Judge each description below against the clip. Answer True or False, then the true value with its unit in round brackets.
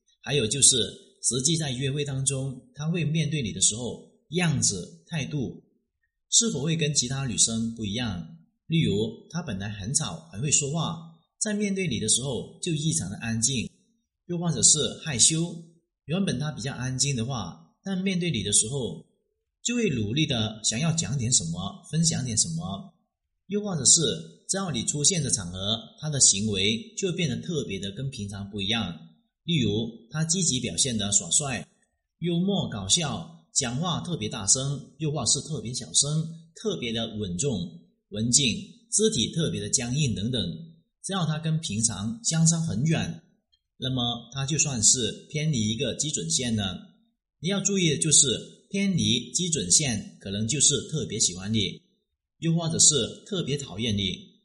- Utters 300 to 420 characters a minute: False (245 characters per minute)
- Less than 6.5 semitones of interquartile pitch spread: False (7.1 semitones)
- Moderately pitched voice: True (145 Hz)